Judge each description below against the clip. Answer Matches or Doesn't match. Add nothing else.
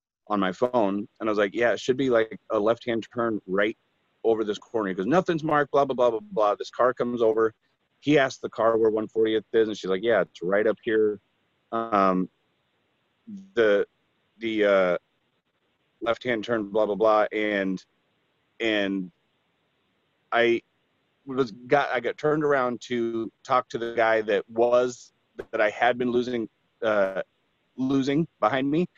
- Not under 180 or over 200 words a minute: Doesn't match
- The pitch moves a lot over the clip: Doesn't match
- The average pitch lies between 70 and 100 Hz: Doesn't match